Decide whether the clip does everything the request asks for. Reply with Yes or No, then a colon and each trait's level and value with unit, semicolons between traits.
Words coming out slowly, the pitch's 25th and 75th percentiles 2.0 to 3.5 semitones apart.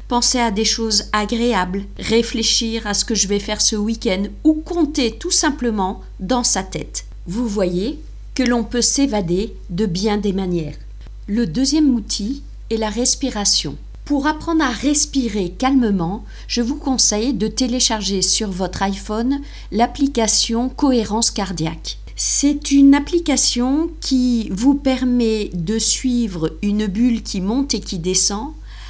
No: slow, 140 wpm; average, 4.3 semitones